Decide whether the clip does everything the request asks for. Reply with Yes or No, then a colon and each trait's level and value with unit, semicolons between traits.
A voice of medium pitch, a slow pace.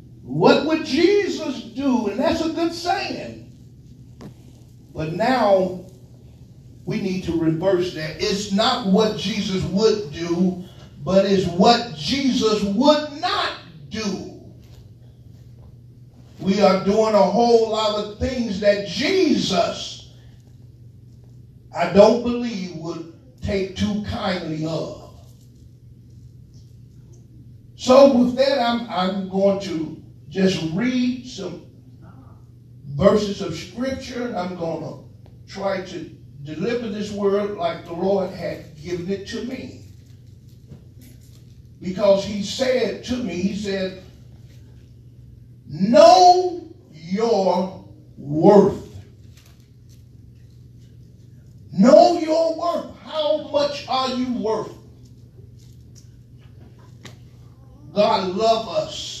Yes: medium, 180 Hz; slow, 100 wpm